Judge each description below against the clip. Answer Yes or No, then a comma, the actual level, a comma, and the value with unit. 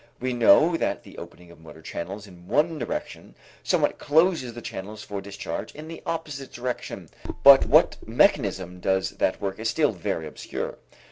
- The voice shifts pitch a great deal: Yes, wide, 7.4 semitones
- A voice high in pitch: No, low, 115 Hz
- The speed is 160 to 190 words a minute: Yes, average, 165 wpm